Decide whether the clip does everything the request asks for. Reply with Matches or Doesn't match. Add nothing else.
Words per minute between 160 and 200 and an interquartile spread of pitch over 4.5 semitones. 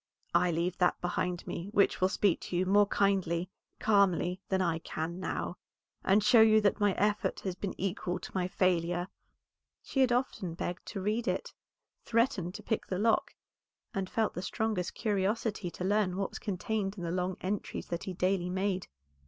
Doesn't match